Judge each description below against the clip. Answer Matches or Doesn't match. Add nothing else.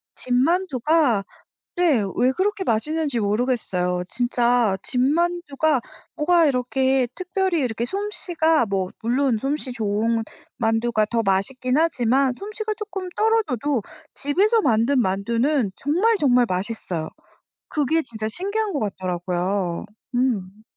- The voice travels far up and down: Matches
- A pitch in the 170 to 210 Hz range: Doesn't match